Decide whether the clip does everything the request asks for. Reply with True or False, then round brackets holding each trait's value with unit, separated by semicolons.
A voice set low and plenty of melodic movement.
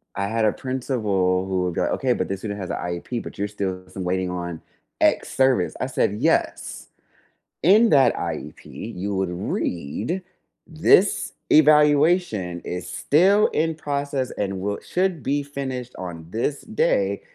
True (115 Hz; 8.1 semitones)